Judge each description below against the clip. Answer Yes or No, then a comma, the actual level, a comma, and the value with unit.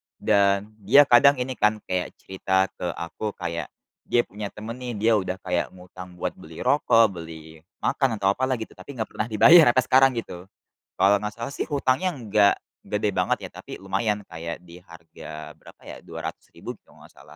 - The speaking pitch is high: No, low, 105 Hz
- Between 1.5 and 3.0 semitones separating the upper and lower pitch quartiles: No, average, 4.9 semitones